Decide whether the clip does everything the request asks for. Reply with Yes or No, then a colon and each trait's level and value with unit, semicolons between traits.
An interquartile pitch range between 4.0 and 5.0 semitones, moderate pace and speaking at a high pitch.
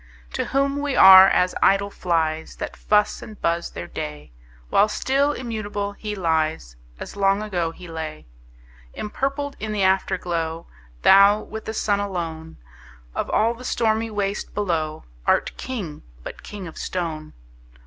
Yes: average, 4.5 semitones; average, 150 wpm; high, 195 Hz